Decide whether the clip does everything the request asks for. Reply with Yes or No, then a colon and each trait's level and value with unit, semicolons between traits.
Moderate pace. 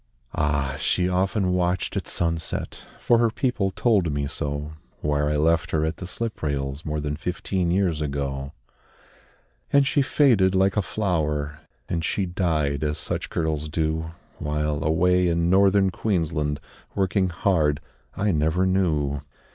Yes: average, 145 wpm